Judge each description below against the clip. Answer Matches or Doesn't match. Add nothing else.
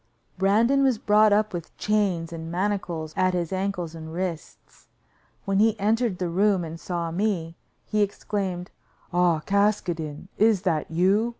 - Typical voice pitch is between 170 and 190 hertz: Matches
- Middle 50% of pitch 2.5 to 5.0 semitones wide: Matches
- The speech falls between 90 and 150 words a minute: Matches